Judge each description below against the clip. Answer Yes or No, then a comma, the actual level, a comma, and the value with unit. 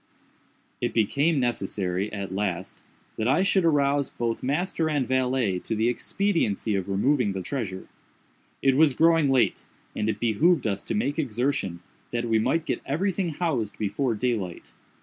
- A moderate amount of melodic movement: No, wide, 5.9 semitones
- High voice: No, low, 125 Hz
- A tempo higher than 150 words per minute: Yes, average, 160 wpm